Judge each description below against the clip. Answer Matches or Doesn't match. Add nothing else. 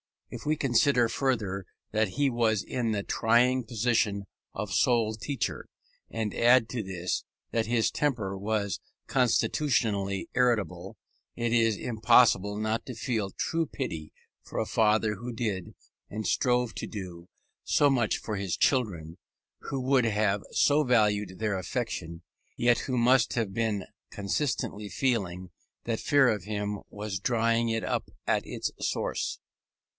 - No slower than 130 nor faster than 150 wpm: Matches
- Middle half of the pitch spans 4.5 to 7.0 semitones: Doesn't match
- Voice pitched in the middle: Doesn't match